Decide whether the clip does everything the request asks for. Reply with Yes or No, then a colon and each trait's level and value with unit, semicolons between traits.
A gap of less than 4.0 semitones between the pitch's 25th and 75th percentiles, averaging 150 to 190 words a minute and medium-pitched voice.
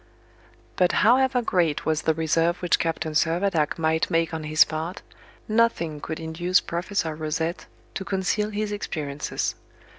No: average, 3.4 semitones; average, 140 wpm; medium, 165 Hz